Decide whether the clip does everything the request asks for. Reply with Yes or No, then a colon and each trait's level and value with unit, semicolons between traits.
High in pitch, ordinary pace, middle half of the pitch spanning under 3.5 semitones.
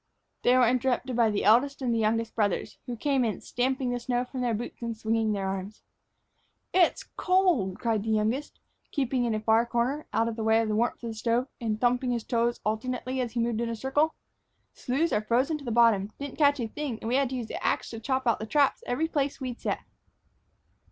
No: high, 240 Hz; fast, 225 wpm; average, 2.8 semitones